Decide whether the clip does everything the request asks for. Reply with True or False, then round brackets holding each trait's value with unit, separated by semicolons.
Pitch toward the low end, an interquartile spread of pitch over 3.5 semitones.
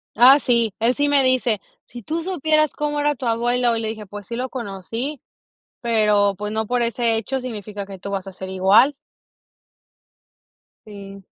False (230 Hz; 4.1 semitones)